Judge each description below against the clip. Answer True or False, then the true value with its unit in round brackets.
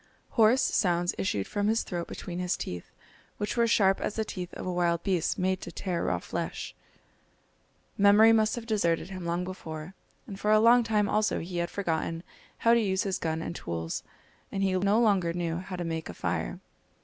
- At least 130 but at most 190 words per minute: False (200 wpm)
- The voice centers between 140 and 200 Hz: True (185 Hz)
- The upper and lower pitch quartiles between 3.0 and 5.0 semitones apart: True (3.6 semitones)